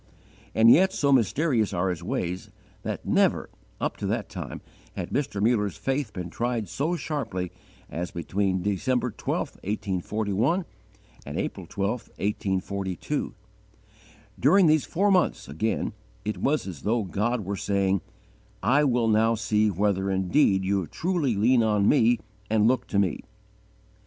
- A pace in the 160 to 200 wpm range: No, average, 140 wpm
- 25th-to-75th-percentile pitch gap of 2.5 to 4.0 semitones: No, average, 5.0 semitones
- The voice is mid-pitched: No, low, 105 Hz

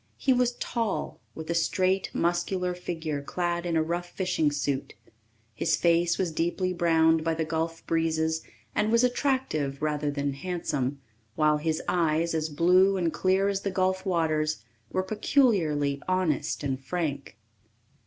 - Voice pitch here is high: No, medium, 170 Hz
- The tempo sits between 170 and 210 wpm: No, average, 150 wpm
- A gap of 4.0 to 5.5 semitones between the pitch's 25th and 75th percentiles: No, average, 3.2 semitones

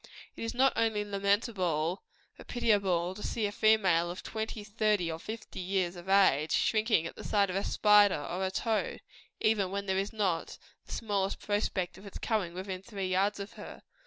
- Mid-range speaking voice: No, high, 200 Hz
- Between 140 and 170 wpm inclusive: No, average, 190 wpm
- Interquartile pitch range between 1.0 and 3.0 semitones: Yes, narrow, 2.5 semitones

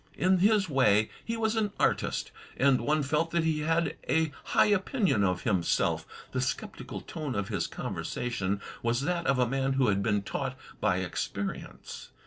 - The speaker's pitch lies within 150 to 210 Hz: No, medium, 140 Hz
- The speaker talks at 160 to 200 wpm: Yes, average, 170 wpm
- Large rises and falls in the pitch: Yes, wide, 7.7 semitones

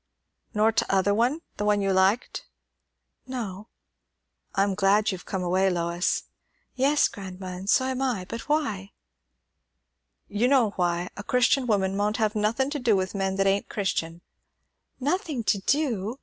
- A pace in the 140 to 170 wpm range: Yes, average, 150 wpm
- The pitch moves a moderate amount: Yes, average, 4.5 semitones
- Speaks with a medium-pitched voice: No, high, 205 Hz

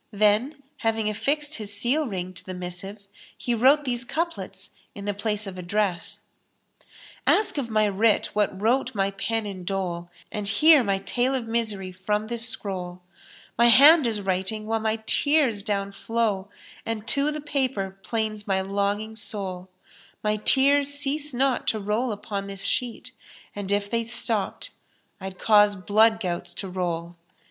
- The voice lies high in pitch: Yes, high, 215 Hz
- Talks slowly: No, average, 165 wpm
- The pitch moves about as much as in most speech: Yes, average, 3.6 semitones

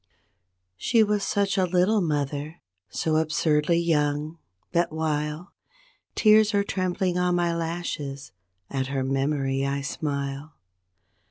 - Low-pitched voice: No, medium, 160 Hz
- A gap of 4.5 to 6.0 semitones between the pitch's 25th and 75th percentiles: No, average, 3.9 semitones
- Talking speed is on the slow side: Yes, slow, 115 wpm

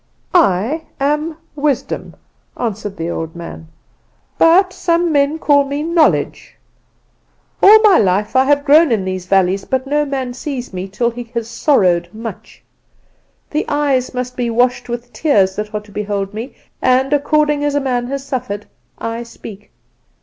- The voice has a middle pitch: No, very high, 250 Hz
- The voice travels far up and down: Yes, wide, 5.8 semitones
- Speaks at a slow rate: No, average, 155 wpm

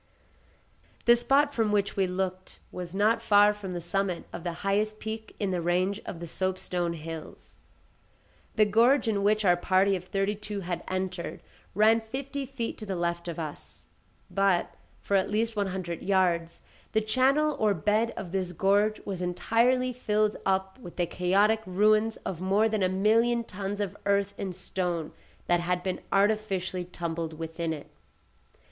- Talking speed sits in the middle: Yes, average, 170 wpm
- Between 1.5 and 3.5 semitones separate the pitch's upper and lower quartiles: Yes, average, 3.2 semitones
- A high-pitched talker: Yes, high, 195 Hz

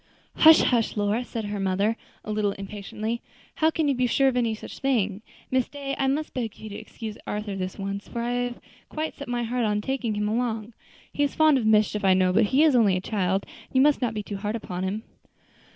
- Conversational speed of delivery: No, fast, 240 wpm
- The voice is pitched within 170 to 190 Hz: No, high, 225 Hz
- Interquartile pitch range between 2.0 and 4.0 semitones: Yes, average, 3.7 semitones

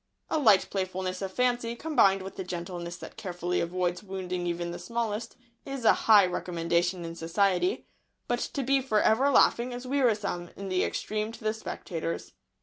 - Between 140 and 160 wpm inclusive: No, average, 170 wpm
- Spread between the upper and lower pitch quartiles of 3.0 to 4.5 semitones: No, average, 4.9 semitones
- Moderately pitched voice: No, high, 195 Hz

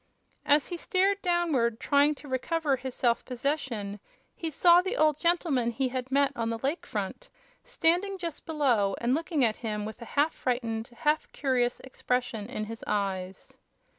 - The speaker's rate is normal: Yes, average, 165 wpm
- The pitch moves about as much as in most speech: No, wide, 5.7 semitones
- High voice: Yes, very high, 265 Hz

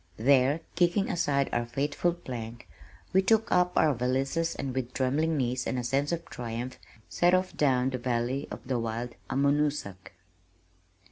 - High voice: No, low, 135 Hz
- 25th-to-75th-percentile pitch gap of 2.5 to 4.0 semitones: No, average, 4.5 semitones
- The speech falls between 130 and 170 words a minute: Yes, average, 155 wpm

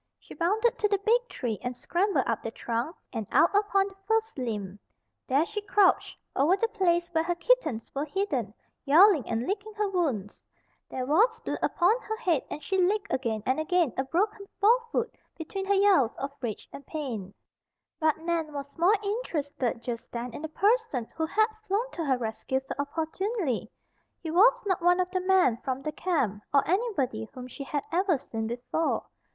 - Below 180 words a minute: No, average, 185 wpm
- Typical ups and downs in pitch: No, wide, 7.5 semitones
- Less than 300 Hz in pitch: No, very high, 330 Hz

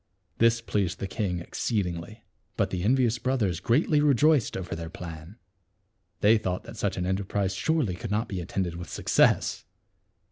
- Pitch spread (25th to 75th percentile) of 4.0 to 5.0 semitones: Yes, average, 4.5 semitones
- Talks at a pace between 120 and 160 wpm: No, average, 170 wpm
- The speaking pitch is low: Yes, low, 100 Hz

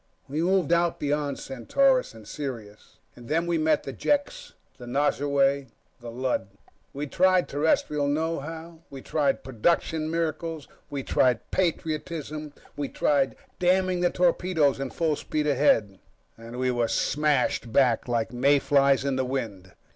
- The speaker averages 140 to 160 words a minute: Yes, average, 145 wpm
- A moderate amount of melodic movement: Yes, average, 3.9 semitones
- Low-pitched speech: No, medium, 145 Hz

